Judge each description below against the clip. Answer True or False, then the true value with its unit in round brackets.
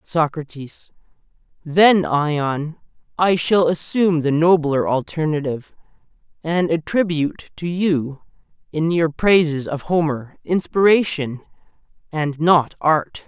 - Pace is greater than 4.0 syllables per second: False (3.9 syllables/s)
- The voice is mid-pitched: True (160 Hz)